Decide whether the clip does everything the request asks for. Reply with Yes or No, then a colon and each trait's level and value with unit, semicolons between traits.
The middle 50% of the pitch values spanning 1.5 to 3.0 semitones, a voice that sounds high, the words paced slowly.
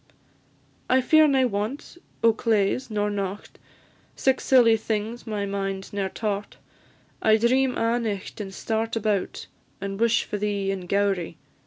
No: average, 2.7 semitones; high, 215 Hz; average, 145 wpm